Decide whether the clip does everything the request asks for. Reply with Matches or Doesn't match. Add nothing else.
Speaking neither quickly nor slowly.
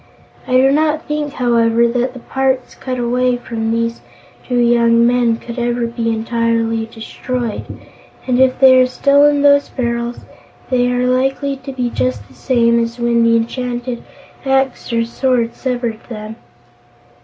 Matches